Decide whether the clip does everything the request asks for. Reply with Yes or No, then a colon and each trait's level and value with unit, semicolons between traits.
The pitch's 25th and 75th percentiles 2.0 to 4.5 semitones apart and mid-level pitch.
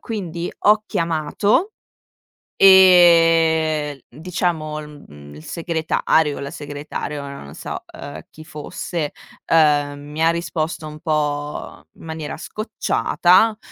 Yes: narrow, 2.6 semitones; medium, 155 Hz